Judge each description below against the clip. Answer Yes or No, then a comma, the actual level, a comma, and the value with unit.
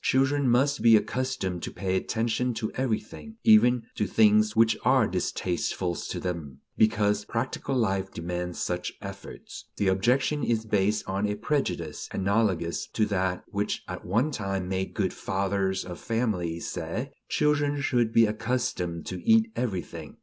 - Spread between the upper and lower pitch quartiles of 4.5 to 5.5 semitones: Yes, average, 4.8 semitones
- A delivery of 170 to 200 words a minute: No, average, 150 wpm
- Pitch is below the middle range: Yes, low, 105 Hz